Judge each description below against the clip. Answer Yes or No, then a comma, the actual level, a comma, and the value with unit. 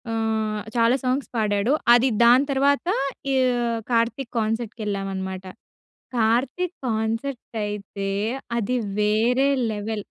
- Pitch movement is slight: No, average, 3.0 semitones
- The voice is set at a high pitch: Yes, high, 225 Hz